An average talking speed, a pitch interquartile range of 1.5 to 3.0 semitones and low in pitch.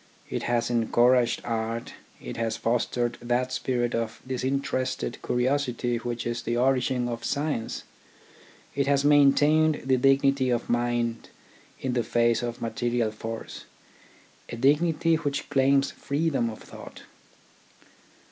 No: slow, 125 wpm; average, 2.7 semitones; low, 125 Hz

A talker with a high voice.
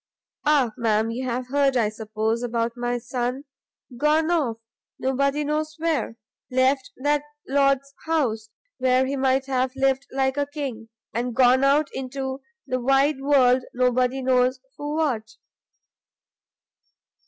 Yes: very high, 260 Hz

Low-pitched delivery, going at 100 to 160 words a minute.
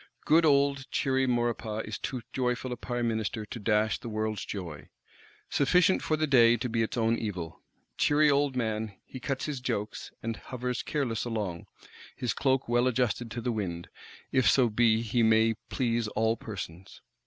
No: low, 115 Hz; average, 170 wpm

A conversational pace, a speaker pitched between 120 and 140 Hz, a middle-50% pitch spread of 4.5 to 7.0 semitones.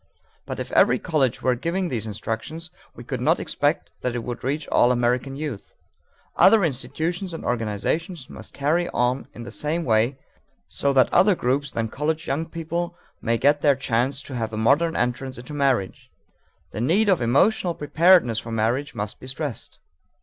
Yes: average, 175 wpm; low, 135 Hz; average, 5.1 semitones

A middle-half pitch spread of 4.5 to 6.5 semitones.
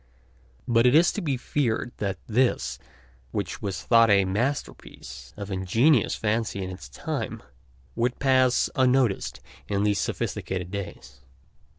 Yes: average, 4.9 semitones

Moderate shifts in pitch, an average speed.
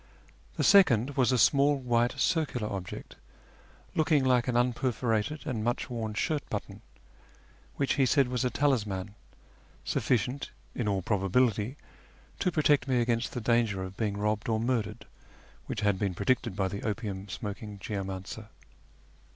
Yes: average, 3.8 semitones; average, 145 wpm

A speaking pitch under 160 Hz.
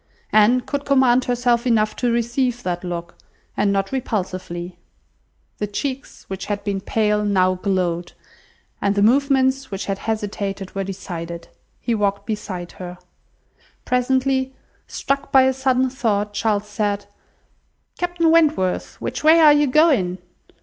No: high, 215 Hz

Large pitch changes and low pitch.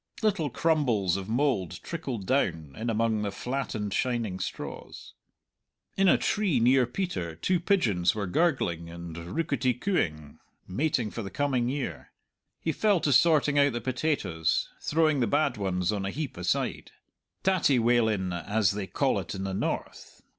Yes: wide, 7.4 semitones; low, 120 Hz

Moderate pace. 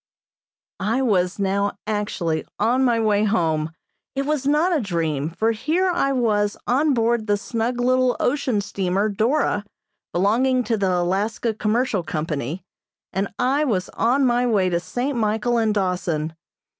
Yes: average, 150 wpm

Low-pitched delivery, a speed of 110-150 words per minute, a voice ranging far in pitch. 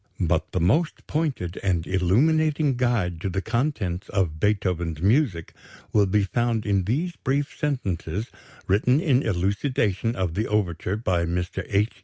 Yes: low, 100 Hz; average, 145 wpm; wide, 6.0 semitones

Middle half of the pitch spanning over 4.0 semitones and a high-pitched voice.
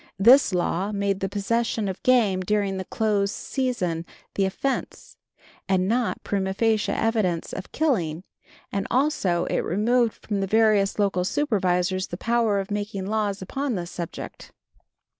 No: average, 3.1 semitones; high, 200 Hz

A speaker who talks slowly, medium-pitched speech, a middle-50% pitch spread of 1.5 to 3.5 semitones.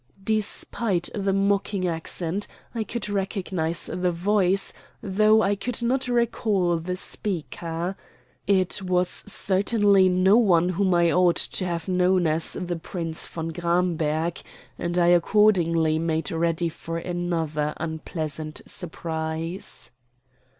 Yes: slow, 120 wpm; medium, 180 Hz; average, 3.0 semitones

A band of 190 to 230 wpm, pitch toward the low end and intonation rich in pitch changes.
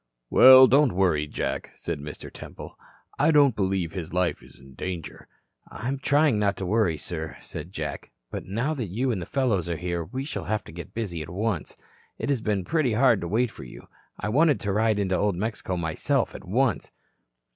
Yes: average, 200 wpm; low, 100 Hz; wide, 6.3 semitones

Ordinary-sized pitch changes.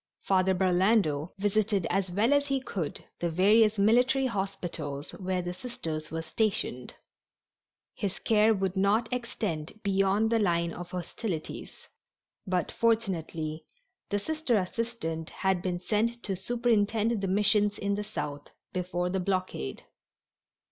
Yes: average, 3.7 semitones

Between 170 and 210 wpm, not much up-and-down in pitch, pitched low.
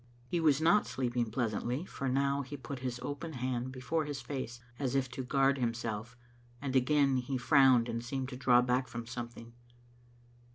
Yes: average, 175 wpm; narrow, 2.3 semitones; low, 130 Hz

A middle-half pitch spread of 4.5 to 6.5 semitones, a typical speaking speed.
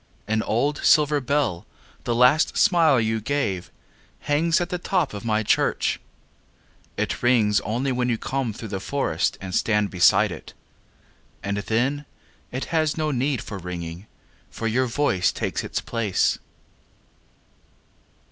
No: wide, 5.5 semitones; slow, 125 wpm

